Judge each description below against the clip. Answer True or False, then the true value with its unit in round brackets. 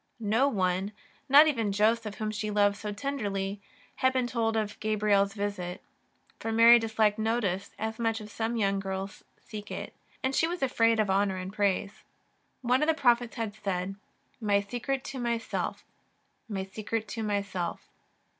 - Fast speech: False (165 wpm)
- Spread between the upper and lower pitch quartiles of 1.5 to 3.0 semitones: True (2.6 semitones)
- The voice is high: True (215 Hz)